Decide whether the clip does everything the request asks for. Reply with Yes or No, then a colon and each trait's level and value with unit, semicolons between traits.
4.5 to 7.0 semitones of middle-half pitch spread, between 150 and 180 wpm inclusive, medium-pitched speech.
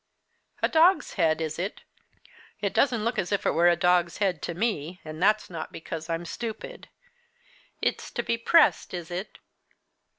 Yes: average, 5.1 semitones; average, 170 wpm; medium, 180 Hz